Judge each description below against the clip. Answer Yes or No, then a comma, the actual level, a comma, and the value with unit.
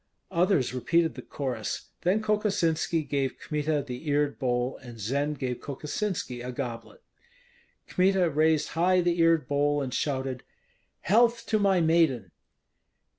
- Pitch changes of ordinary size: Yes, average, 4.9 semitones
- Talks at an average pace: No, slow, 130 wpm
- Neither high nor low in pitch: Yes, medium, 150 Hz